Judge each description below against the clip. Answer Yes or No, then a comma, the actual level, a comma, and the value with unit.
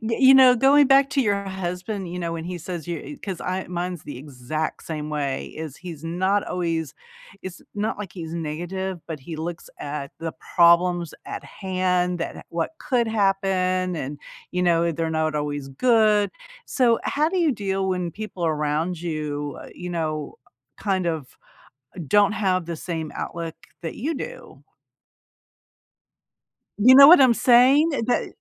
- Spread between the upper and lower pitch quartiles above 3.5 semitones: Yes, average, 4.4 semitones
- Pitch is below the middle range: No, medium, 180 Hz